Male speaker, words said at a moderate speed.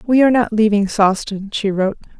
No: female; average, 190 wpm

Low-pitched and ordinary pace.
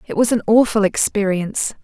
No: high, 210 Hz; average, 165 wpm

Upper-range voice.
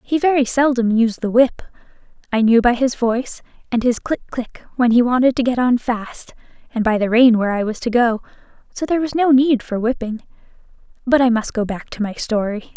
Yes: high, 240 Hz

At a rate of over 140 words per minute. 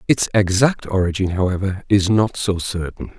Yes: average, 150 wpm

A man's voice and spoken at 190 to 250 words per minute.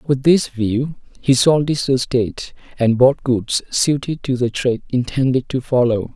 No: male; average, 165 wpm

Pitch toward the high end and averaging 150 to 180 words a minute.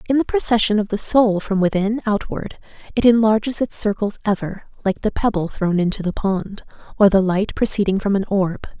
No: high, 205 Hz; average, 190 wpm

